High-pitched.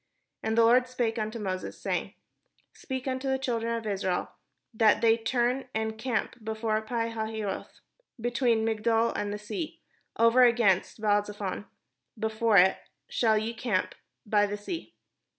Yes: high, 225 Hz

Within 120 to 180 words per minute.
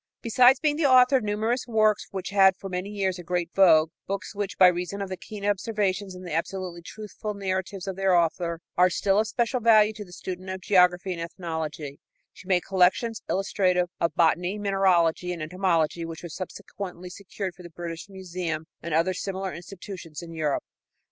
No: average, 190 wpm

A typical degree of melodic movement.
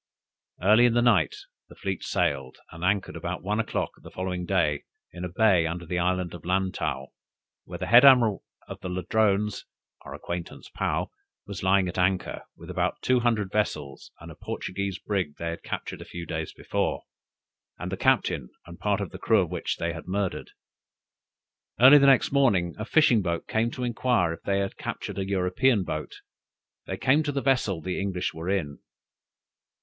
Yes: average, 4.1 semitones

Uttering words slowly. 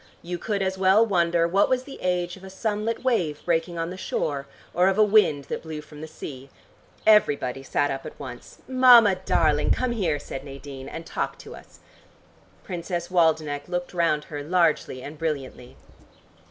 No: average, 180 wpm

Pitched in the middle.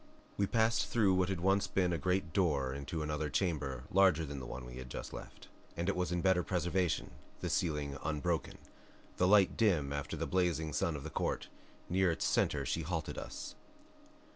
No: very low, 85 Hz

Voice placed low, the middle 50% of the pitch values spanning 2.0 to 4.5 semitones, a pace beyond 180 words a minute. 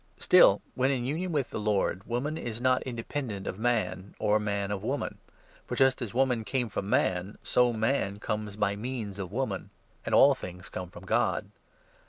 Yes: low, 110 Hz; average, 4.2 semitones; average, 195 wpm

